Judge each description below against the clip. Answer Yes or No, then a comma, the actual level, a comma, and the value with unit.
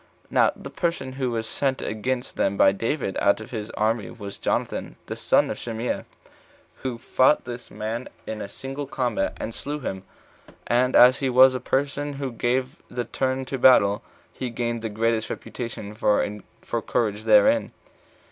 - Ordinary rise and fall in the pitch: Yes, average, 3.1 semitones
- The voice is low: Yes, low, 120 Hz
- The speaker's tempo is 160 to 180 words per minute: Yes, average, 170 wpm